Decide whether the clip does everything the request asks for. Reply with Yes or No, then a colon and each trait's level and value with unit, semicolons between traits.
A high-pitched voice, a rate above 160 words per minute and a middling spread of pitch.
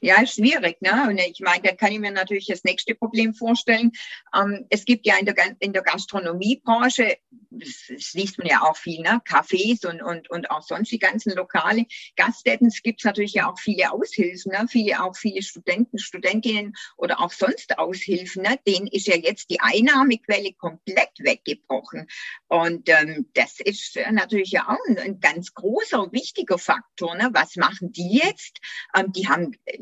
Yes: high, 205 Hz; average, 175 wpm; average, 3.7 semitones